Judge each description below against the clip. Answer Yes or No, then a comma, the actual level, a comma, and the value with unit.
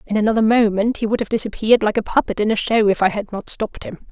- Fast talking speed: Yes, fast, 275 wpm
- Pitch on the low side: No, high, 215 Hz